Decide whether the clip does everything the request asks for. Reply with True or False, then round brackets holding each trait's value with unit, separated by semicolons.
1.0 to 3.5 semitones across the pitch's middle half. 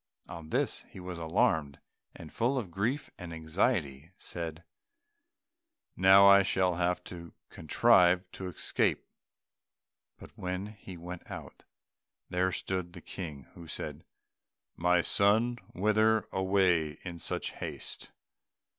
True (2.8 semitones)